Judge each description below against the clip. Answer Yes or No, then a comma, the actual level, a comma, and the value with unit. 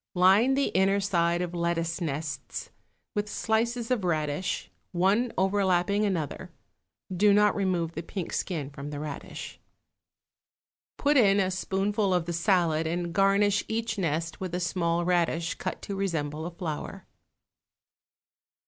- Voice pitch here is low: No, medium, 180 Hz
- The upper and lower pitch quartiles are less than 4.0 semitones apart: Yes, average, 3.2 semitones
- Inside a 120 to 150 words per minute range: Yes, average, 140 wpm